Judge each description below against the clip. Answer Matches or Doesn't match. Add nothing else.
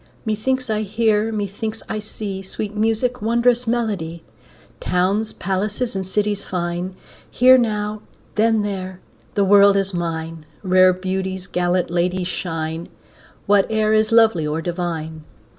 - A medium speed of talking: Doesn't match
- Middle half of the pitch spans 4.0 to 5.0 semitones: Doesn't match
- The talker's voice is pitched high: Matches